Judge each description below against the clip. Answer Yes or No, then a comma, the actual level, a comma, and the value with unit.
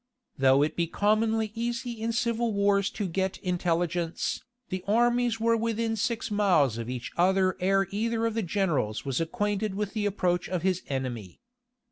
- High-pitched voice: Yes, high, 200 Hz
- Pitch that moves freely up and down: No, average, 4.5 semitones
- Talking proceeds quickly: No, average, 165 wpm